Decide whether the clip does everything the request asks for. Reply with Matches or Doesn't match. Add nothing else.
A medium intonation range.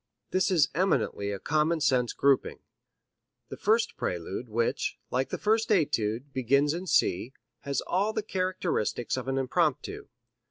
Doesn't match